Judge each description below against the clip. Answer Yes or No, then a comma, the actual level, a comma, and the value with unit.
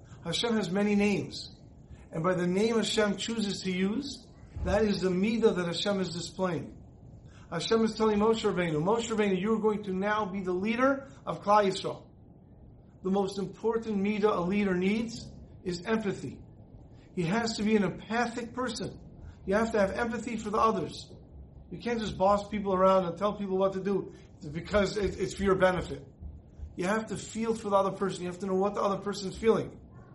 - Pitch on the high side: Yes, high, 195 Hz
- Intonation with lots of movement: No, average, 2.9 semitones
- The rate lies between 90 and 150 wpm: No, average, 195 wpm